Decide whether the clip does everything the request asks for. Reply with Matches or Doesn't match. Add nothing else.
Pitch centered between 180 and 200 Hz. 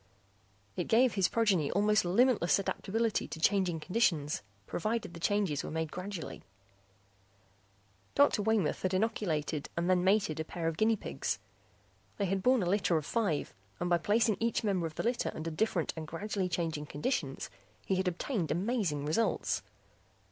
Matches